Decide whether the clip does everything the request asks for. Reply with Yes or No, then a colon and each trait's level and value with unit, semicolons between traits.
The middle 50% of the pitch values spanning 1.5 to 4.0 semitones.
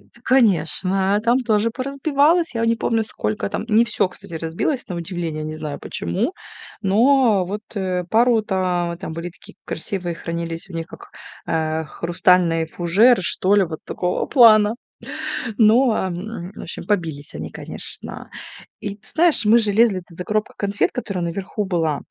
No: average, 4.9 semitones